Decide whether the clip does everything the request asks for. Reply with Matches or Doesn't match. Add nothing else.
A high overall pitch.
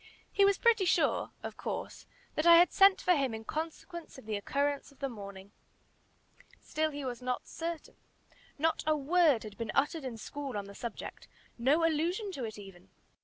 Matches